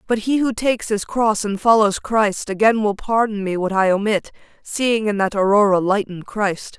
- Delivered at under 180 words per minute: No, average, 195 wpm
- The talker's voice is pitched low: No, high, 210 Hz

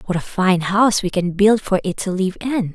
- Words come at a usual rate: No, fast, 265 wpm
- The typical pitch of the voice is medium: No, high, 195 Hz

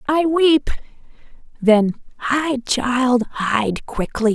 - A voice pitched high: Yes, very high, 255 Hz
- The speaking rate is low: Yes, slow, 95 wpm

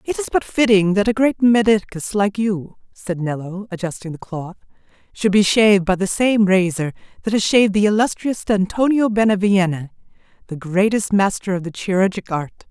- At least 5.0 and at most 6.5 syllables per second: Yes, 5.2 syllables/s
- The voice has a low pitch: No, high, 200 Hz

